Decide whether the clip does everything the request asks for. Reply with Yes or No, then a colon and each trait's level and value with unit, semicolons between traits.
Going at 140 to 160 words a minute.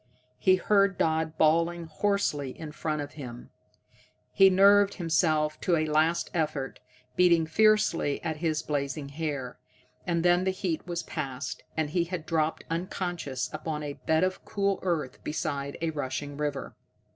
Yes: average, 150 wpm